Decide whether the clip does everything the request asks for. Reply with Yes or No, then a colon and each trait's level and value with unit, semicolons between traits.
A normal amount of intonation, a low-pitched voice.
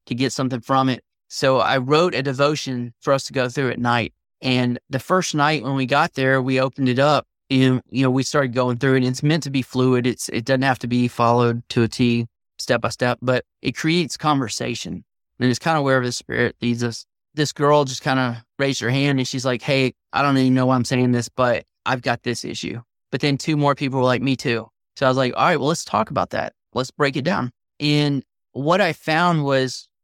No: narrow, 2.2 semitones; low, 130 Hz